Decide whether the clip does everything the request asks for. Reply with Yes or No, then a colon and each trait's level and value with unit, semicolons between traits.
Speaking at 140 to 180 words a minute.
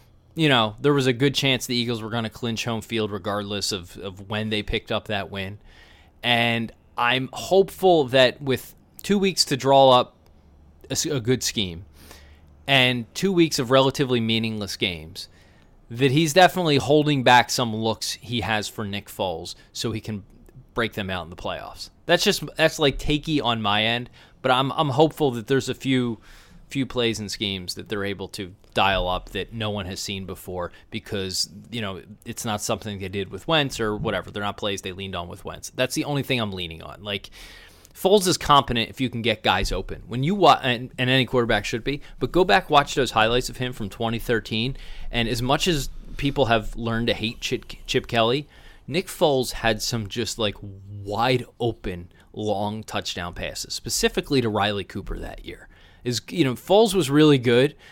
No: average, 195 wpm